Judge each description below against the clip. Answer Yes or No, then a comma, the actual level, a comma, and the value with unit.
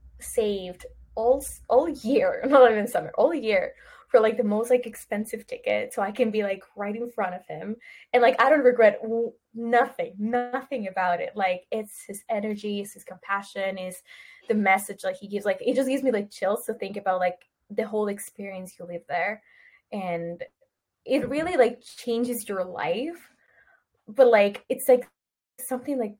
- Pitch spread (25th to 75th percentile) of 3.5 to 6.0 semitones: Yes, average, 4.1 semitones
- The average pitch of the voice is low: No, high, 220 Hz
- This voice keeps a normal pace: Yes, average, 180 wpm